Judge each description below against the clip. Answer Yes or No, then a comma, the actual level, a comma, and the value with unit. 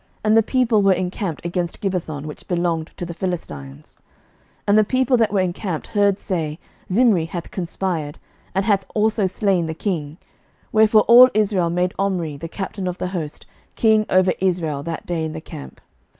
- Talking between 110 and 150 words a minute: No, average, 180 wpm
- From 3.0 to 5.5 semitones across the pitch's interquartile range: Yes, average, 3.8 semitones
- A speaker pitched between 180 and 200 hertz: Yes, medium, 185 Hz